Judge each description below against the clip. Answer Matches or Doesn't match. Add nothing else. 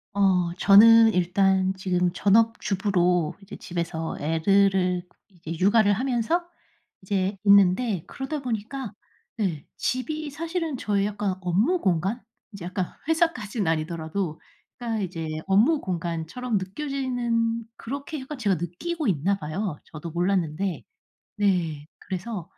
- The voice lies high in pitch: Matches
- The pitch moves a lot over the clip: Doesn't match